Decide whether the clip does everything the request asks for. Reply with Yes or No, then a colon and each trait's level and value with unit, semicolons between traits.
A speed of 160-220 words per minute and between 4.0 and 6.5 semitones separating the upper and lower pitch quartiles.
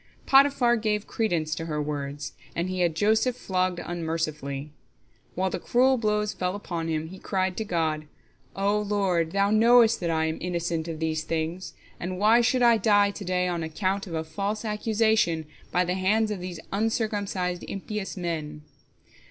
Yes: average, 170 wpm; average, 4.4 semitones